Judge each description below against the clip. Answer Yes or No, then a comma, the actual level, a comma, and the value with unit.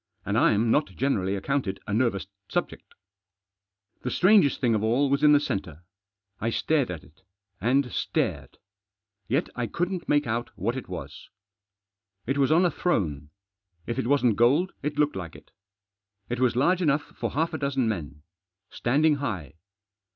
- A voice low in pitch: Yes, low, 125 Hz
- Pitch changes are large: Yes, wide, 5.9 semitones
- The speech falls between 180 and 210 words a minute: No, average, 165 wpm